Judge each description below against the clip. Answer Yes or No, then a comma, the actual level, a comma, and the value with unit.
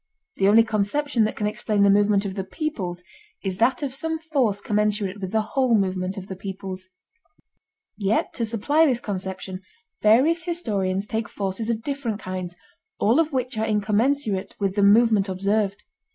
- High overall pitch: Yes, high, 210 Hz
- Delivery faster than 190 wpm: No, average, 165 wpm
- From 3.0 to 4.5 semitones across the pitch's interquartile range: Yes, average, 3.6 semitones